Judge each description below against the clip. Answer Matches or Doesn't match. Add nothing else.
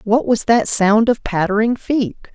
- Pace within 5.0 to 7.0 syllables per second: Doesn't match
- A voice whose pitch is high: Matches